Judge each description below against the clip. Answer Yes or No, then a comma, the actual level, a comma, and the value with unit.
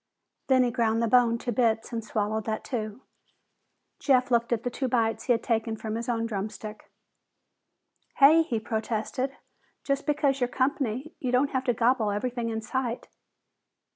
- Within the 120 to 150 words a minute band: No, average, 170 wpm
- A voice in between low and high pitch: No, high, 235 Hz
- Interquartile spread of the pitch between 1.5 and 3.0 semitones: Yes, narrow, 2.6 semitones